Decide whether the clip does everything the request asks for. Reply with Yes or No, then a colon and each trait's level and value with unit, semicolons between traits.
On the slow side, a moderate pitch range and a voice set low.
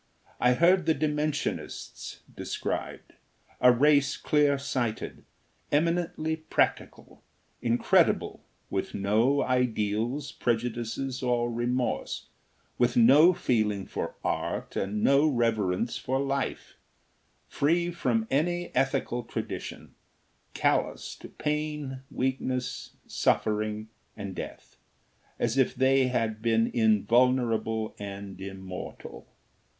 Yes: slow, 95 wpm; average, 4.2 semitones; low, 125 Hz